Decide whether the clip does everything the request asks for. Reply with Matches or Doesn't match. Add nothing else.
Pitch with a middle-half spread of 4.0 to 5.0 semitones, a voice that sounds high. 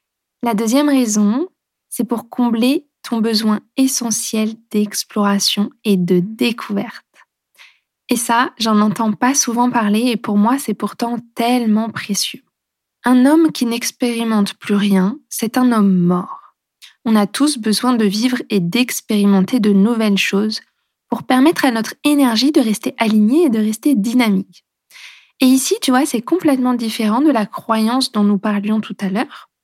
Doesn't match